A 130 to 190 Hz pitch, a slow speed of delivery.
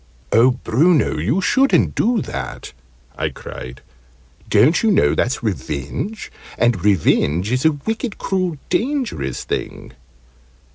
Yes: low, 135 Hz; slow, 115 wpm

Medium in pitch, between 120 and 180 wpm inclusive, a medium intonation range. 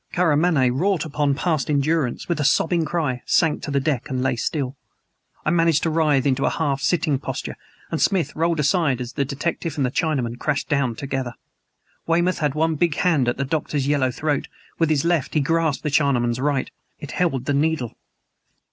No: medium, 145 Hz; average, 190 wpm; average, 3.3 semitones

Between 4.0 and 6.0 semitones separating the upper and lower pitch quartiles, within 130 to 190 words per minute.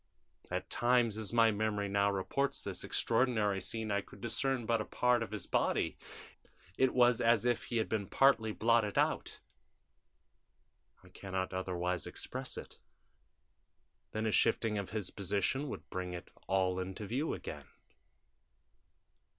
No: average, 3.4 semitones; average, 150 wpm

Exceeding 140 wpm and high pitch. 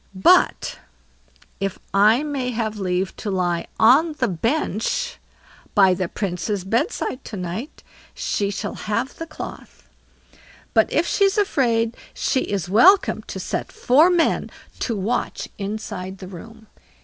No: slow, 135 wpm; high, 220 Hz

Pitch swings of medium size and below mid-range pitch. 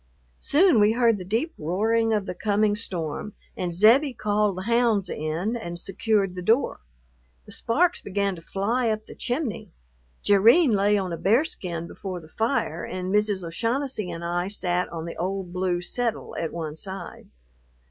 No: average, 4.3 semitones; high, 200 Hz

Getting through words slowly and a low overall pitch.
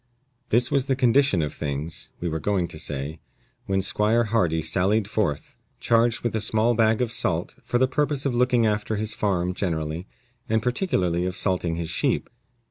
No: average, 180 wpm; low, 105 Hz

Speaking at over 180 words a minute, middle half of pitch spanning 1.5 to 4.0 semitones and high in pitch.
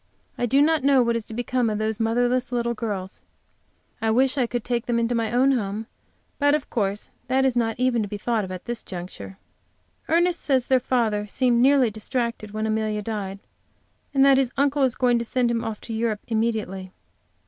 Yes: fast, 205 wpm; average, 2.9 semitones; high, 235 Hz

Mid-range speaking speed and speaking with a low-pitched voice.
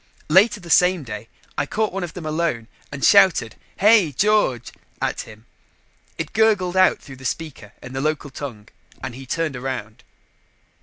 No: average, 165 wpm; medium, 155 Hz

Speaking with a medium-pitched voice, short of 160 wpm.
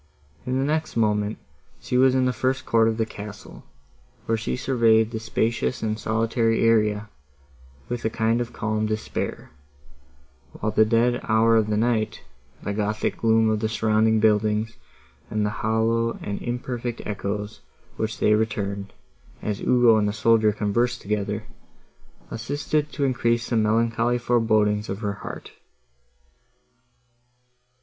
No: low, 110 Hz; average, 140 wpm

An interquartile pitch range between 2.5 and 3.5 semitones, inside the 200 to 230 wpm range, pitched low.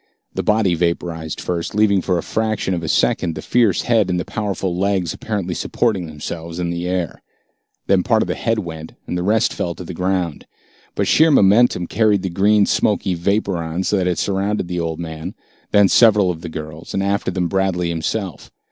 Yes: average, 3.1 semitones; fast, 205 wpm; very low, 90 Hz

